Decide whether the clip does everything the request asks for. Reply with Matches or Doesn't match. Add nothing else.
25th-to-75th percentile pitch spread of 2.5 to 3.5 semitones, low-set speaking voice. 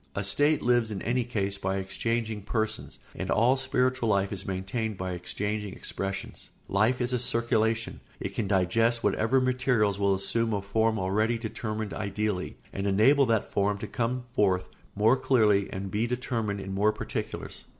Matches